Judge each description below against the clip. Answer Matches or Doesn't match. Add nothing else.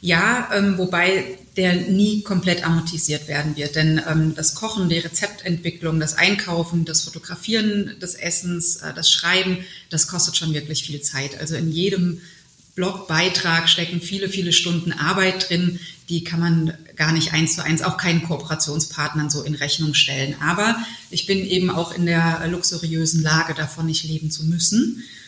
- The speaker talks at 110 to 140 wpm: Doesn't match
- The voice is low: Doesn't match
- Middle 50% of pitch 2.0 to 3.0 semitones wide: Matches